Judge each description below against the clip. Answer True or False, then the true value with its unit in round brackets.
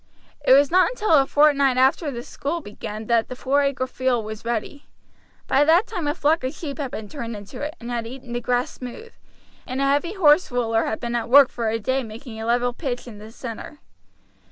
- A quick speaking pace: True (225 wpm)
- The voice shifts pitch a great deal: False (3.6 semitones)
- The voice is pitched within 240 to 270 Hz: True (255 Hz)